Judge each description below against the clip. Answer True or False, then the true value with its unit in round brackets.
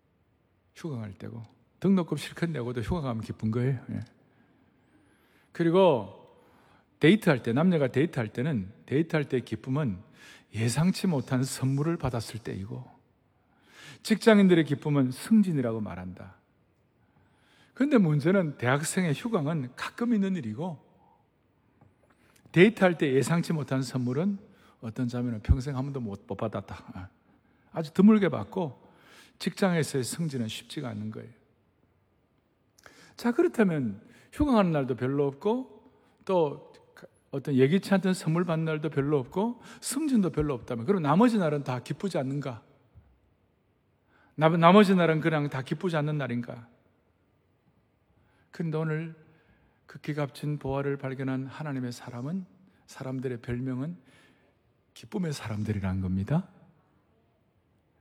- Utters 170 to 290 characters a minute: True (270 characters per minute)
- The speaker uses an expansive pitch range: True (6.1 semitones)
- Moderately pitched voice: True (145 Hz)